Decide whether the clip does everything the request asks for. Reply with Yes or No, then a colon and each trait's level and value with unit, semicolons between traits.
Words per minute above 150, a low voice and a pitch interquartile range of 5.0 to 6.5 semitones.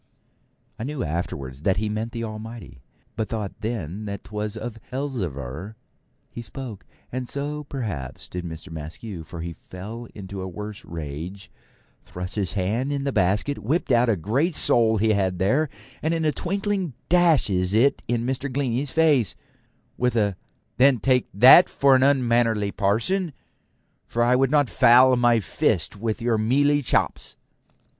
Yes: average, 160 wpm; low, 115 Hz; average, 5.3 semitones